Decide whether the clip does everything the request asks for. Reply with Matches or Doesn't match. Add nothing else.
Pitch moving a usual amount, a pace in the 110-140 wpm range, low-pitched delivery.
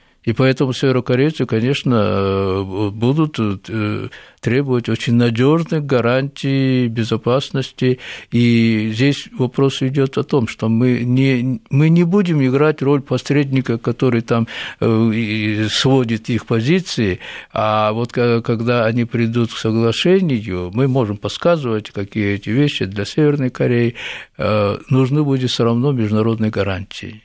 Matches